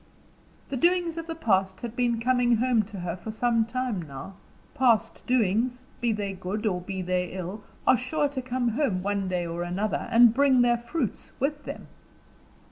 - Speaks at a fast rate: No, average, 185 wpm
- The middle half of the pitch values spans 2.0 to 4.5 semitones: No, average, 5.0 semitones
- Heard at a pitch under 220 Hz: No, high, 230 Hz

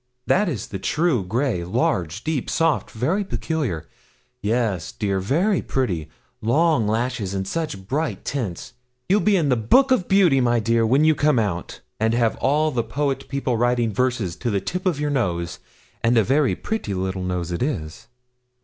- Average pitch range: No, wide, 7.3 semitones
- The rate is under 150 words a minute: No, average, 175 wpm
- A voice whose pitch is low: Yes, low, 120 Hz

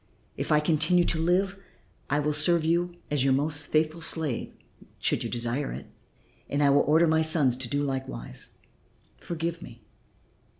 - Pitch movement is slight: No, average, 3.0 semitones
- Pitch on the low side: No, medium, 150 Hz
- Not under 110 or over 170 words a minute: Yes, average, 165 wpm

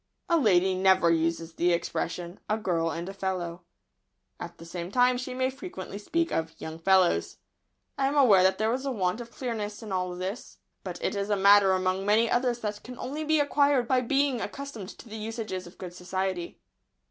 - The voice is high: Yes, high, 200 Hz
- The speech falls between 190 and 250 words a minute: Yes, average, 200 wpm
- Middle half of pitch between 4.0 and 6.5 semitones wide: Yes, wide, 5.5 semitones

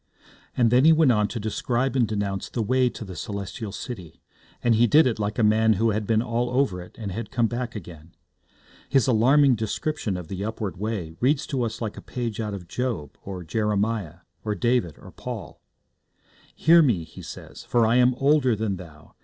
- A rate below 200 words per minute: No, fast, 205 wpm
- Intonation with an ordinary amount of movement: Yes, average, 3.8 semitones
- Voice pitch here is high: No, low, 110 Hz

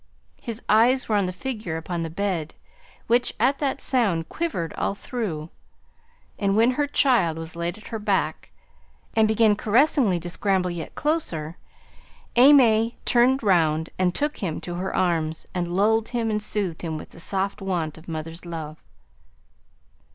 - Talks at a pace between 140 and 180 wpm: Yes, average, 160 wpm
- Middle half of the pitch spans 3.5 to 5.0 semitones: No, wide, 5.6 semitones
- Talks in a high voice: Yes, high, 195 Hz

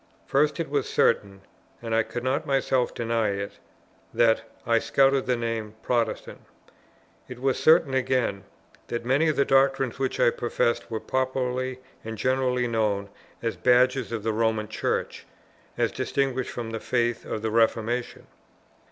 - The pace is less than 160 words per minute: Yes, average, 150 wpm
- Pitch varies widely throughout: No, average, 2.7 semitones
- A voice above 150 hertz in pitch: No, low, 120 Hz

